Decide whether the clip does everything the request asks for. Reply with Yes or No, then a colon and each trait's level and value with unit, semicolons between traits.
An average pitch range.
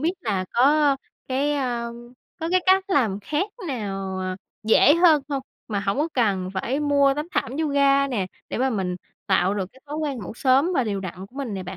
No: wide, 6.5 semitones